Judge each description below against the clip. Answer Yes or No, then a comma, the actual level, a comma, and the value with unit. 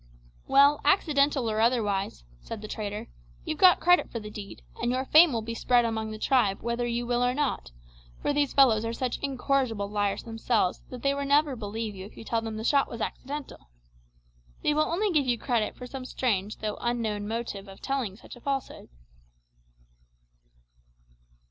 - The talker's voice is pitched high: Yes, high, 240 Hz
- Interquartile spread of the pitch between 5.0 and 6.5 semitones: No, average, 4.2 semitones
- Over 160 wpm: Yes, average, 185 wpm